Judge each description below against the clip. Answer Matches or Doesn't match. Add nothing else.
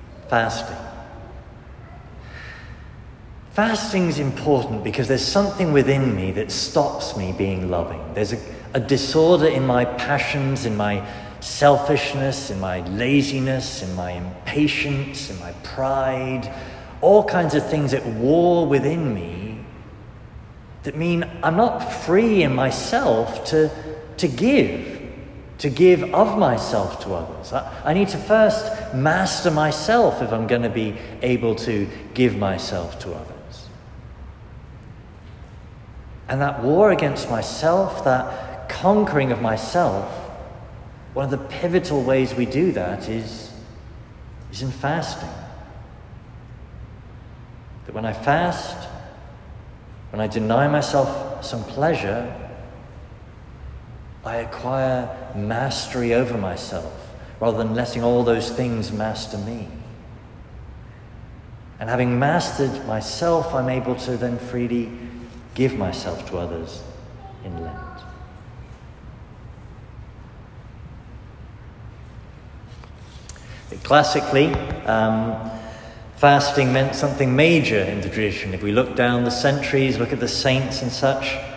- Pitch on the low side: Matches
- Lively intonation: Doesn't match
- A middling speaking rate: Doesn't match